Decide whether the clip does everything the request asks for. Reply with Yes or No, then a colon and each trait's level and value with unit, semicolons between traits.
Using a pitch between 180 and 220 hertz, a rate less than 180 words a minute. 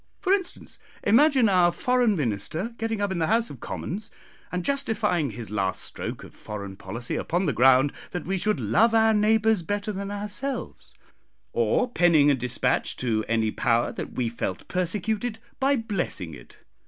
Yes: medium, 185 Hz; average, 165 wpm